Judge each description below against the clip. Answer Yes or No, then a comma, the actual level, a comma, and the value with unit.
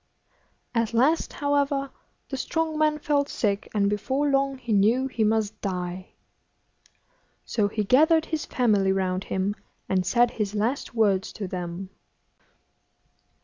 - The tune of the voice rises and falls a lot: Yes, wide, 5.8 semitones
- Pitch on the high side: Yes, high, 225 Hz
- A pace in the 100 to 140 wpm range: Yes, slow, 135 wpm